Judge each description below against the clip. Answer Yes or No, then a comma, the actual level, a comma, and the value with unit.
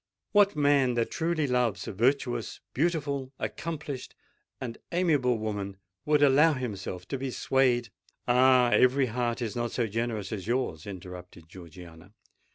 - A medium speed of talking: No, slow, 125 wpm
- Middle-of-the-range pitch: No, low, 125 Hz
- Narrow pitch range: No, average, 4.9 semitones